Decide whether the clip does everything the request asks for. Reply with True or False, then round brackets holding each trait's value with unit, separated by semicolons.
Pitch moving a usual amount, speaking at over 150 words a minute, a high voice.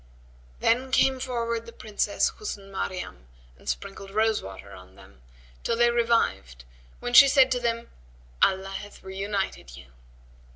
False (4.1 semitones; 140 wpm; 210 Hz)